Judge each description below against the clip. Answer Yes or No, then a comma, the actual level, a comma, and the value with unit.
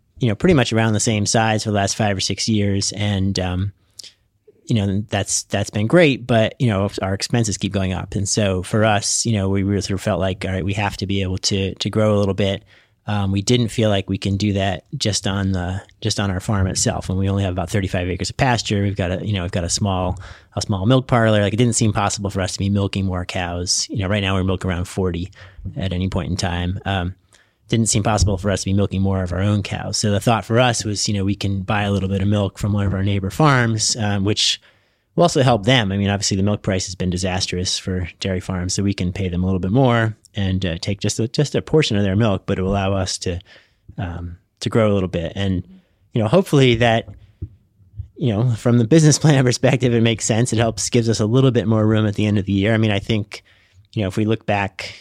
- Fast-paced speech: Yes, fast, 270 wpm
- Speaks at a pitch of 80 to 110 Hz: Yes, low, 100 Hz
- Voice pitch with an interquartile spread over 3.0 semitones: No, narrow, 2.5 semitones